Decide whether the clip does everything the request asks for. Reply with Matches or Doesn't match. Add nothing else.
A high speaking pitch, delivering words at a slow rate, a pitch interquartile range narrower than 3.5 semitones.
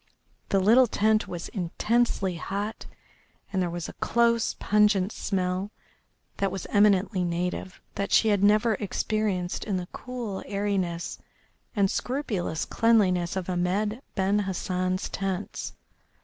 Matches